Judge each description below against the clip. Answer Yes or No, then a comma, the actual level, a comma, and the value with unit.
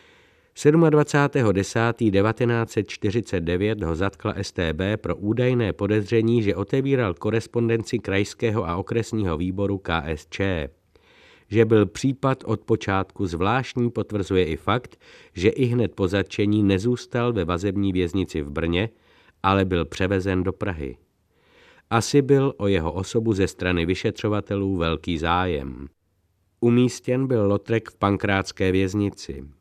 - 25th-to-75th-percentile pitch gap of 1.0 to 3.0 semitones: No, average, 3.7 semitones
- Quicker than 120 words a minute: No, slow, 115 wpm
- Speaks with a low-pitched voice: Yes, low, 100 Hz